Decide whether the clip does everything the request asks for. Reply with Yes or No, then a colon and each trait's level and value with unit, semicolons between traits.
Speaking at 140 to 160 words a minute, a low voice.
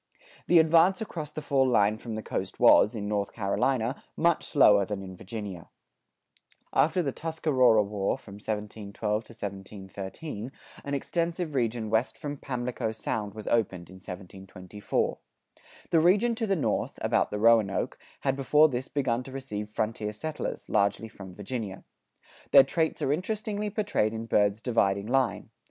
Yes: average, 145 wpm; low, 115 Hz